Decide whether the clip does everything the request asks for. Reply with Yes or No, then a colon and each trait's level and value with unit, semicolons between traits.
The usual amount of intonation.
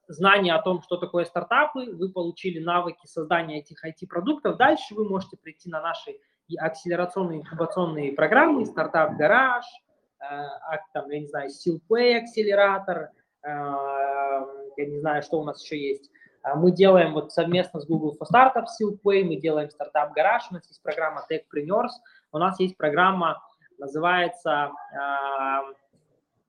Yes: average, 4.5 semitones